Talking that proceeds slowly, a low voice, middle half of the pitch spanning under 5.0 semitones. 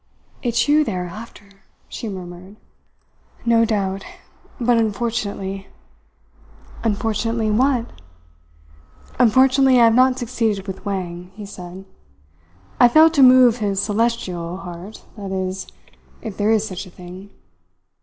No: slow, 125 wpm; high, 210 Hz; average, 3.7 semitones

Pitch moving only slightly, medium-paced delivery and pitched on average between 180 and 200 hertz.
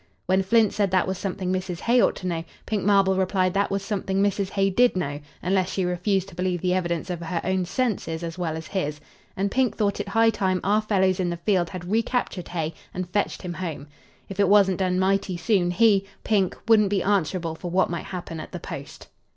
No: narrow, 2.1 semitones; fast, 225 wpm; high, 190 Hz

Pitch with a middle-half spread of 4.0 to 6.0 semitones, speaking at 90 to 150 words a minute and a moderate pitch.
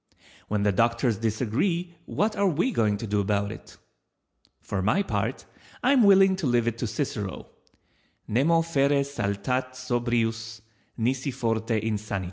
No: average, 5.2 semitones; average, 145 wpm; low, 120 Hz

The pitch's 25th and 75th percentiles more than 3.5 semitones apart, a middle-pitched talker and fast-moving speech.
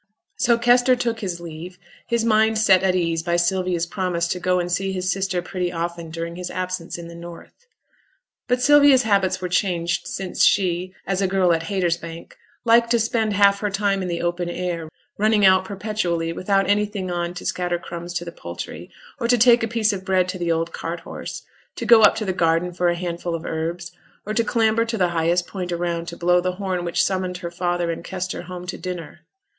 No: average, 2.8 semitones; medium, 180 Hz; fast, 215 wpm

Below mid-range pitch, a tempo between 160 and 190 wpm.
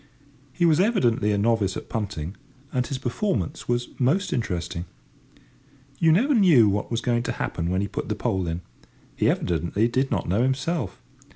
Yes: low, 115 Hz; average, 175 wpm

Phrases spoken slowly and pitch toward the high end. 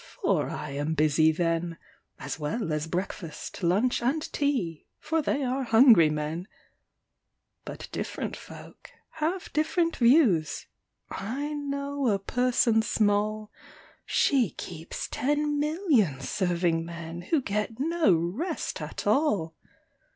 Yes: slow, 120 wpm; high, 215 Hz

